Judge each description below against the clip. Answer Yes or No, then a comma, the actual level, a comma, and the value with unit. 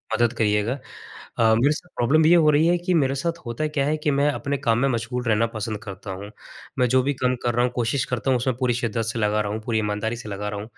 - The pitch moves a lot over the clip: No, average, 4.1 semitones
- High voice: No, low, 120 Hz